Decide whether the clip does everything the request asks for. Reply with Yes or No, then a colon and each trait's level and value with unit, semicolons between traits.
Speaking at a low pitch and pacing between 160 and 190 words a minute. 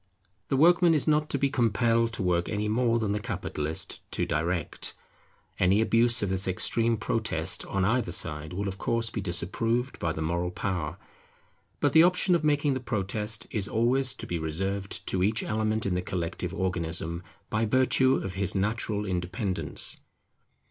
Yes: low, 105 Hz; average, 170 wpm